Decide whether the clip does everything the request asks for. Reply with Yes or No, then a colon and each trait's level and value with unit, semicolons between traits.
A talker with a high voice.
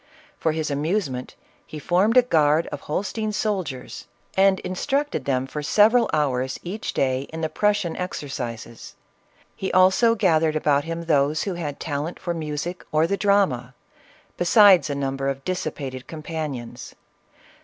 No: medium, 160 Hz